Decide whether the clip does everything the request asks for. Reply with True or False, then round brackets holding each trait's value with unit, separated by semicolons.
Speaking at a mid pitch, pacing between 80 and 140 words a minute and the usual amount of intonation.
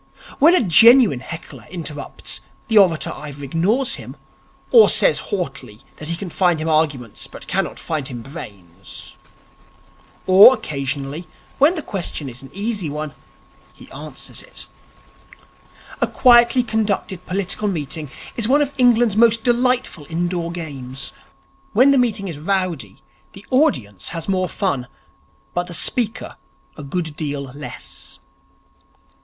False (175 Hz; 135 wpm; 7.3 semitones)